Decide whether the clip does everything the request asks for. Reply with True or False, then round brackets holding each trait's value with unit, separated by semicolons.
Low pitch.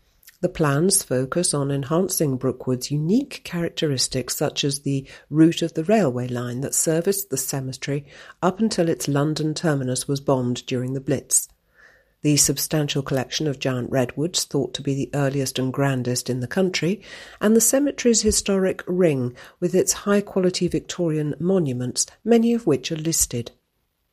False (150 Hz)